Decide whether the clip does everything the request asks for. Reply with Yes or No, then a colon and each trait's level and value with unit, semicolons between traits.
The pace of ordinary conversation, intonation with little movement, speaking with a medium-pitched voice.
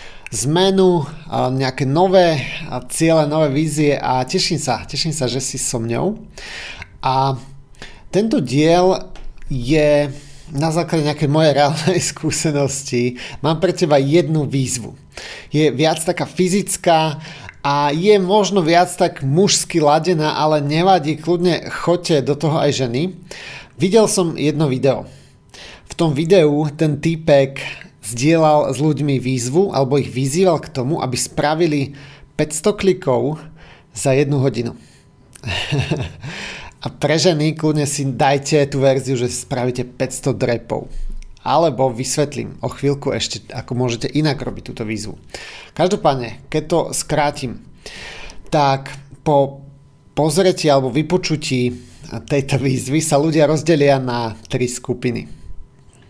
No: average, 120 wpm; average, 3.3 semitones; medium, 145 Hz